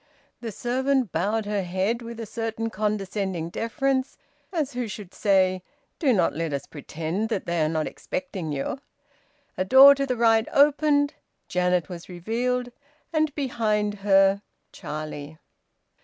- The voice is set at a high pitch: Yes, high, 215 Hz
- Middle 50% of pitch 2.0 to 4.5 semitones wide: No, wide, 5.6 semitones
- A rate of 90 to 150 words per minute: Yes, average, 140 wpm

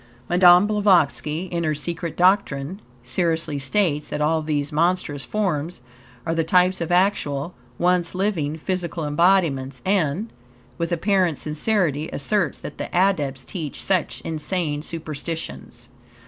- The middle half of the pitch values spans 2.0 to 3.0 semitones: No, average, 3.7 semitones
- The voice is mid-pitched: Yes, medium, 165 Hz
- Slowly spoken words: Yes, slow, 125 wpm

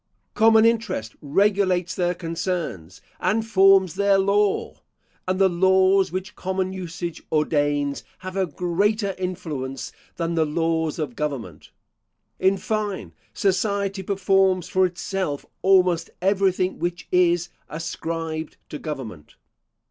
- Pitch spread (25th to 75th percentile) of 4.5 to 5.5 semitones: No, average, 3.1 semitones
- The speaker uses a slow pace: Yes, slow, 115 wpm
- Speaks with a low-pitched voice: No, medium, 185 Hz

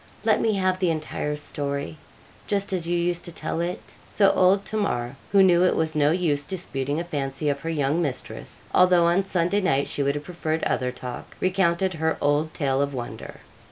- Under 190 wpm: No, average, 195 wpm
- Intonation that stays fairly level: No, average, 4.2 semitones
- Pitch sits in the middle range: Yes, medium, 165 Hz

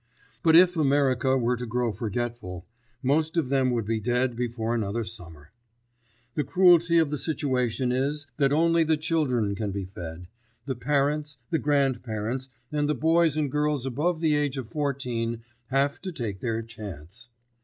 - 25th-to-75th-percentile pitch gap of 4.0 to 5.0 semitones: Yes, average, 4.6 semitones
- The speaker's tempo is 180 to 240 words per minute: No, average, 165 wpm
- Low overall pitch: Yes, low, 130 Hz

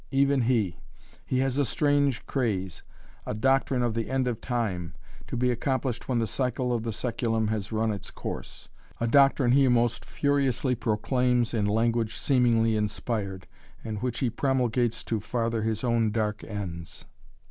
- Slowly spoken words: No, average, 160 wpm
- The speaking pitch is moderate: No, low, 120 Hz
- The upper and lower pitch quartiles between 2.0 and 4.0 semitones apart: Yes, average, 2.8 semitones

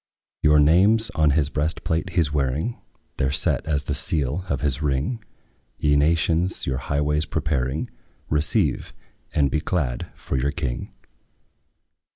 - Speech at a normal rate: Yes, average, 145 wpm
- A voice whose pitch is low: Yes, very low, 75 Hz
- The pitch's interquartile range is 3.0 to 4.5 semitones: No, narrow, 2.6 semitones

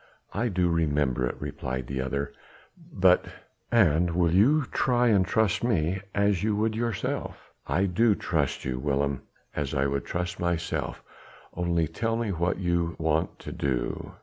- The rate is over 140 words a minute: Yes, average, 155 wpm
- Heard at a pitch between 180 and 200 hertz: No, very low, 85 Hz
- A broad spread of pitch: Yes, wide, 5.8 semitones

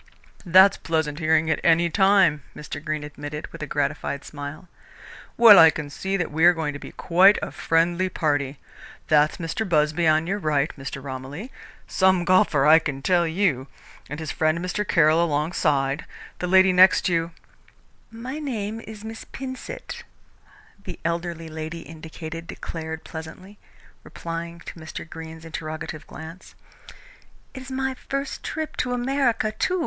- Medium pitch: Yes, medium, 165 Hz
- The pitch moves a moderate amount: Yes, average, 3.8 semitones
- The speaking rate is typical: Yes, average, 155 wpm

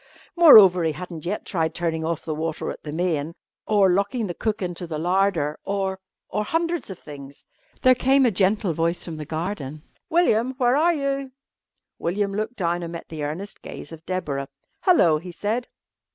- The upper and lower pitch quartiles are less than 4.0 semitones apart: No, average, 5.0 semitones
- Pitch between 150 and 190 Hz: Yes, medium, 185 Hz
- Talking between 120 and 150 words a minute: No, average, 180 wpm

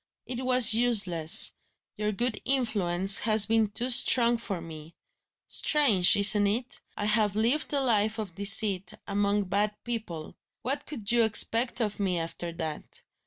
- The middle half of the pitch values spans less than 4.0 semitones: Yes, average, 3.4 semitones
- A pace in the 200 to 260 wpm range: No, average, 150 wpm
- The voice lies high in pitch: Yes, high, 210 Hz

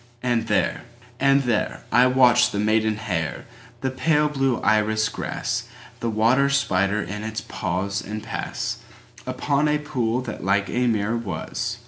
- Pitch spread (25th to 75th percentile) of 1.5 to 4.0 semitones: Yes, average, 3.6 semitones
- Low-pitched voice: Yes, low, 115 Hz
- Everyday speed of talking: No, slow, 125 wpm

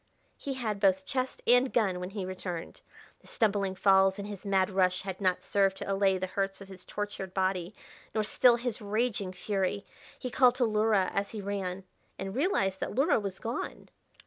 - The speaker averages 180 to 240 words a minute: Yes, average, 190 wpm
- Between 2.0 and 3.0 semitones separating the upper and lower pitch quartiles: Yes, narrow, 2.4 semitones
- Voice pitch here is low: No, high, 195 Hz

